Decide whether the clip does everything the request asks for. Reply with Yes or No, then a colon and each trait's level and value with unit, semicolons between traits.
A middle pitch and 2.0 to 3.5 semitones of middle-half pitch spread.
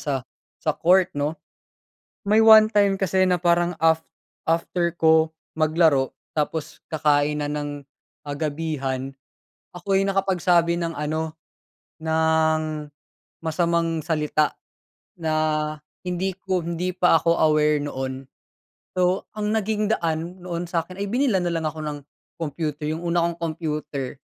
Yes: medium, 165 Hz; average, 2.8 semitones